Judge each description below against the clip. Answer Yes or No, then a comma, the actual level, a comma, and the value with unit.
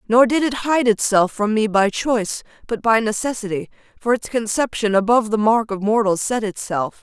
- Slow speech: No, average, 190 wpm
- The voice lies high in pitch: Yes, high, 220 Hz